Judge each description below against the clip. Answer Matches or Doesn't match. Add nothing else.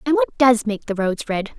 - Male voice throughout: Doesn't match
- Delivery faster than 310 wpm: Doesn't match